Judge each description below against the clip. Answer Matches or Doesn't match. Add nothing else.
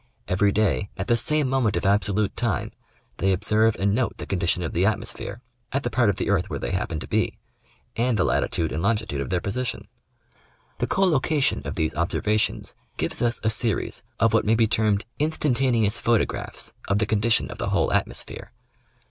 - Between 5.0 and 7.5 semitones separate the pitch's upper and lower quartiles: Doesn't match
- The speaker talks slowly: Doesn't match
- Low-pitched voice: Matches